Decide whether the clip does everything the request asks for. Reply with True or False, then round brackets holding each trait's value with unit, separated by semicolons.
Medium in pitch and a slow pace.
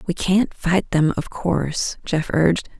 False (175 Hz; 170 wpm)